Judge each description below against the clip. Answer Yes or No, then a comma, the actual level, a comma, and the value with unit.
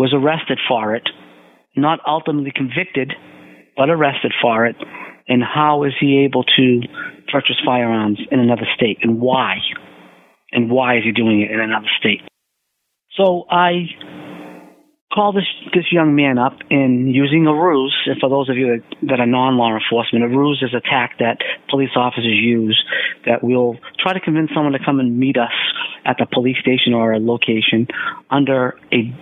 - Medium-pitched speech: No, low, 130 Hz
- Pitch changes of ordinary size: Yes, average, 3.7 semitones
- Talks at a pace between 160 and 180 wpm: Yes, average, 170 wpm